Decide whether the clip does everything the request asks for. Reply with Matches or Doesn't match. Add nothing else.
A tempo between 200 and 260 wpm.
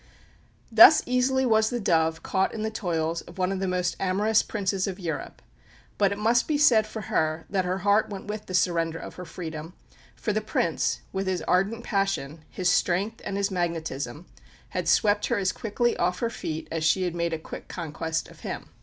Matches